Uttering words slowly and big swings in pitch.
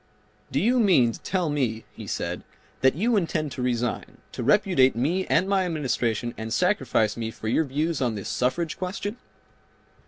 No: average, 175 wpm; wide, 7.3 semitones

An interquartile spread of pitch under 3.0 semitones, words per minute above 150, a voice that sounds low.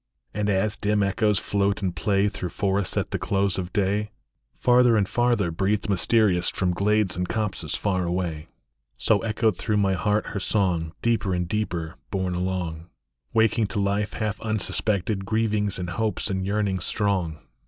Yes: narrow, 2.6 semitones; average, 165 wpm; low, 100 Hz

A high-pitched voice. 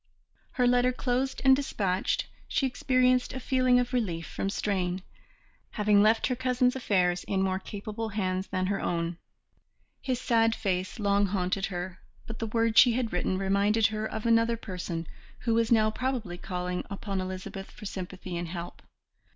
Yes: high, 210 Hz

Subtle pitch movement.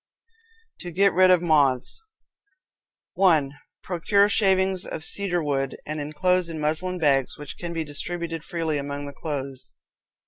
No: average, 3.8 semitones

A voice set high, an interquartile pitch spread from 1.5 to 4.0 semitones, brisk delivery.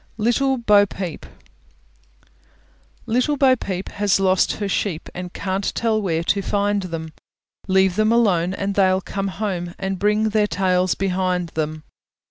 No: high, 195 Hz; narrow, 2.5 semitones; average, 145 wpm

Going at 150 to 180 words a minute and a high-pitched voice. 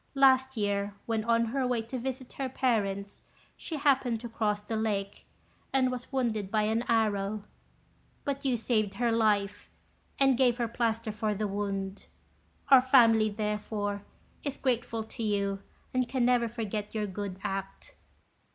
Yes: average, 155 wpm; high, 225 Hz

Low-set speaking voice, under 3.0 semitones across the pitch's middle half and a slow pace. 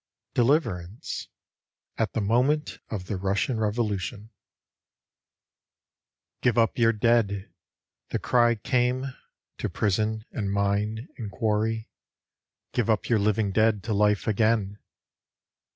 Yes: low, 110 Hz; narrow, 2.4 semitones; slow, 120 wpm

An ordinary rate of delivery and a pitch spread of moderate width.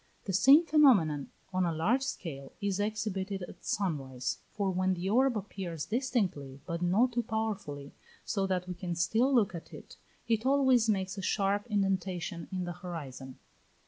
Yes: average, 170 wpm; average, 4.3 semitones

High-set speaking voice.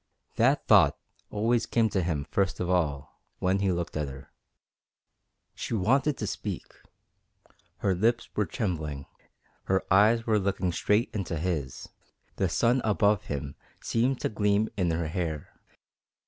No: very low, 95 Hz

